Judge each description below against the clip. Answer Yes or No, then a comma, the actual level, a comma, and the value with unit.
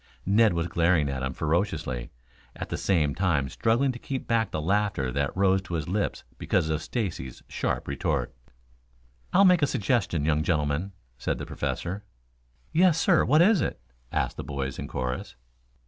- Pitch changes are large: Yes, wide, 7.5 semitones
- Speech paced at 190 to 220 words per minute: No, average, 170 wpm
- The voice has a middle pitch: No, very low, 90 Hz